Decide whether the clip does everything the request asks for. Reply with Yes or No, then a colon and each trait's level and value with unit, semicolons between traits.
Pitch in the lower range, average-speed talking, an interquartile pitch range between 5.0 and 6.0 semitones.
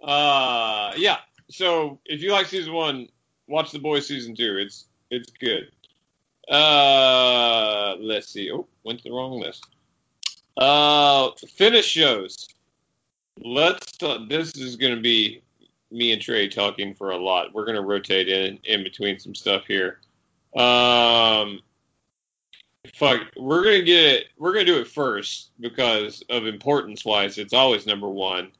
Yes: low, 120 Hz; average, 145 wpm; wide, 5.5 semitones